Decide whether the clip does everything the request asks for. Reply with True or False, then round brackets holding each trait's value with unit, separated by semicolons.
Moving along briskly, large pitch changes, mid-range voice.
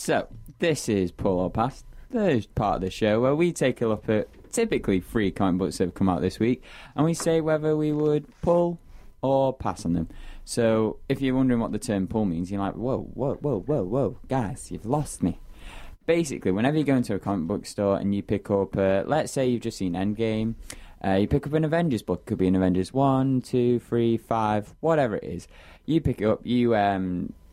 False (225 wpm; 5.8 semitones; 110 Hz)